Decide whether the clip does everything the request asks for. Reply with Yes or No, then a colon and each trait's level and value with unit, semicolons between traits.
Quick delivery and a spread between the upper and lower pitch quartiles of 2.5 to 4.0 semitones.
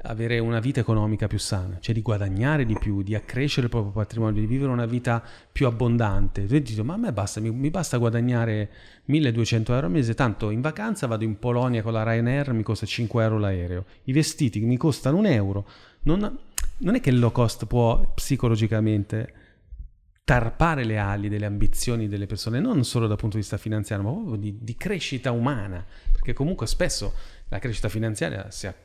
Yes: fast, 195 wpm; average, 2.8 semitones